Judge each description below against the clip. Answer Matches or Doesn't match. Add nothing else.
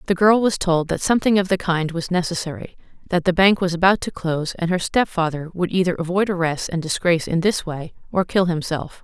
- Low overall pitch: Doesn't match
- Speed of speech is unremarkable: Doesn't match